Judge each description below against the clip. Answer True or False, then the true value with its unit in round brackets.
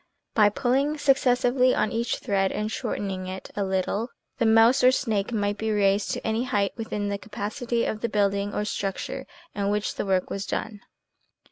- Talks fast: False (180 wpm)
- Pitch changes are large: False (3.0 semitones)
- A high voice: True (210 Hz)